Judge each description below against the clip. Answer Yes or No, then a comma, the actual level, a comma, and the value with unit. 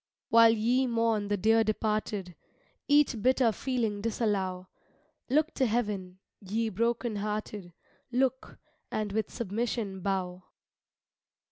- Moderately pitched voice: No, high, 215 Hz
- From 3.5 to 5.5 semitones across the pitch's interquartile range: No, average, 2.7 semitones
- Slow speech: Yes, slow, 110 wpm